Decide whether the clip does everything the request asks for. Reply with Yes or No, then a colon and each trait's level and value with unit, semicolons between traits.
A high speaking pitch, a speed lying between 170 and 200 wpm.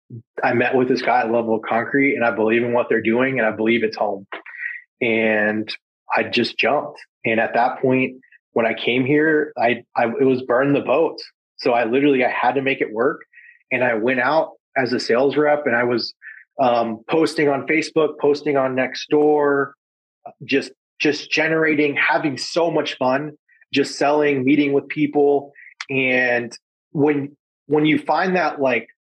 No: medium, 140 Hz; average, 175 wpm